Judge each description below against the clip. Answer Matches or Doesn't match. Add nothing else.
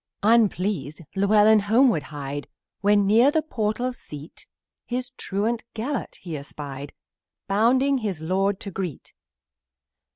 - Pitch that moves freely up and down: Matches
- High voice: Matches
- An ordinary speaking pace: Doesn't match